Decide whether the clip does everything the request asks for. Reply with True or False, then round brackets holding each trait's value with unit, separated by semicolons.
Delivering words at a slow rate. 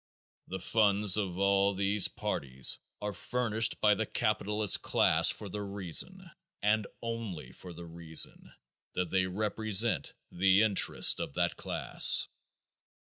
True (125 wpm)